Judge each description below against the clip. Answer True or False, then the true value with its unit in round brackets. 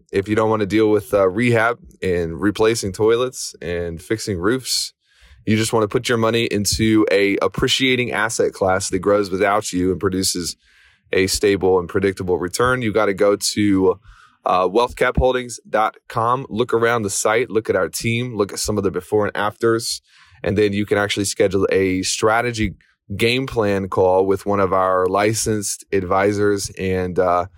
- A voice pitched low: True (105 Hz)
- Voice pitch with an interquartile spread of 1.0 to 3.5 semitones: True (3.0 semitones)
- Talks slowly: False (175 wpm)